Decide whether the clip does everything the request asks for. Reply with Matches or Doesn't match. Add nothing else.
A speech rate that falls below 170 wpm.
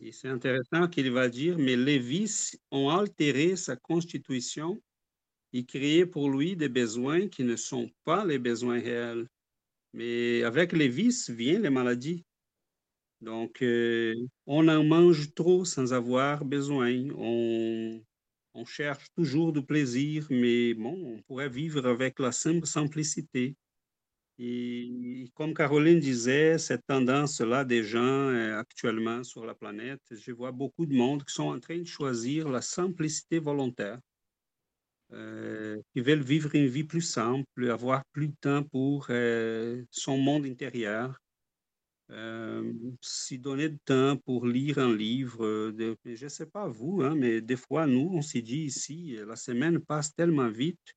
Matches